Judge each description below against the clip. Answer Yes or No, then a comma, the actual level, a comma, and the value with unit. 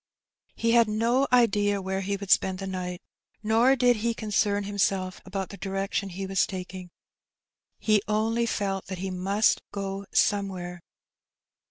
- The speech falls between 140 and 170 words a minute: Yes, average, 150 wpm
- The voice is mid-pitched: No, high, 200 Hz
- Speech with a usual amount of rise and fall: No, narrow, 2.2 semitones